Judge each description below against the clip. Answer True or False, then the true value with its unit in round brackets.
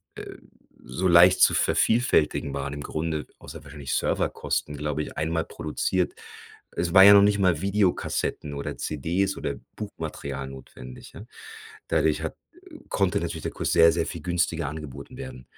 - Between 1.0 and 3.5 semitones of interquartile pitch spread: False (4.4 semitones)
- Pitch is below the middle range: True (80 Hz)